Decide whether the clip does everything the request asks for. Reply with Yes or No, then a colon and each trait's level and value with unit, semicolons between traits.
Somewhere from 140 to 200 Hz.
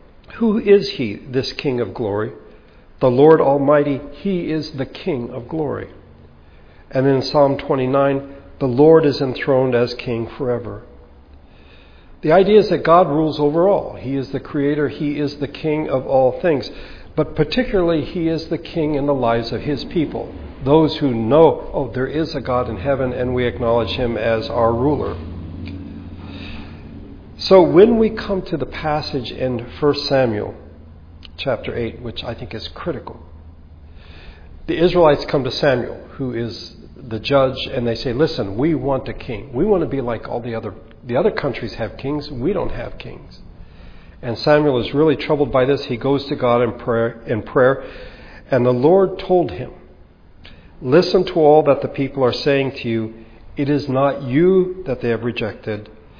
No: low, 130 Hz